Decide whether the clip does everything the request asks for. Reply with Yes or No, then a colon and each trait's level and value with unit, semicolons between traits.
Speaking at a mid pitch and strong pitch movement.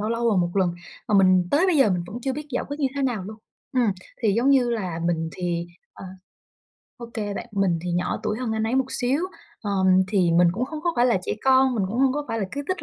No: high, 225 Hz; wide, 6.0 semitones